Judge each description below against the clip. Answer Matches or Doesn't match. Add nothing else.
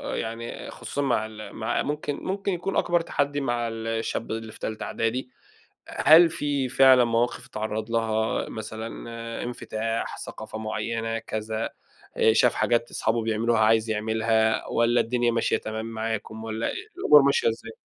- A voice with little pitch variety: Matches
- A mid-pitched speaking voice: Doesn't match